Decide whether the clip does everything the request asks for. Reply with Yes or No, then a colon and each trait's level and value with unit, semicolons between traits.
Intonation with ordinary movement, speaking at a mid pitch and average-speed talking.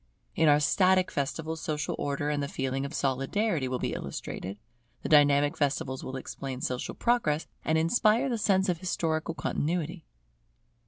Yes: average, 4.1 semitones; medium, 150 Hz; average, 155 wpm